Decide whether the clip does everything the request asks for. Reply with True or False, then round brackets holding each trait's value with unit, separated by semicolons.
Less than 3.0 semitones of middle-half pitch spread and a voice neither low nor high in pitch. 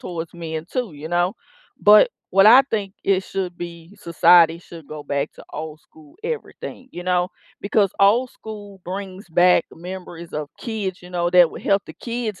False (3.4 semitones; 180 Hz)